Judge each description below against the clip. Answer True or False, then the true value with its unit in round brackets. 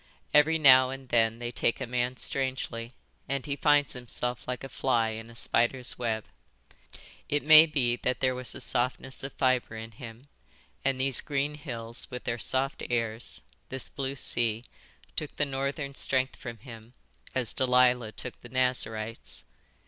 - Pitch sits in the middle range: False (125 Hz)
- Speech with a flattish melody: True (2.3 semitones)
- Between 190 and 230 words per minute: False (165 wpm)